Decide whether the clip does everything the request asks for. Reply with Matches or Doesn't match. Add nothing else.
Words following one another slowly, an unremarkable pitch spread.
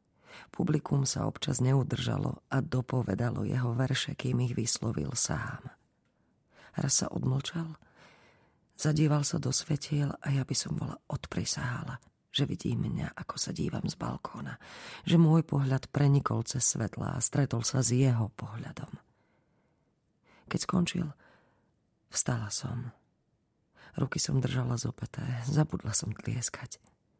Doesn't match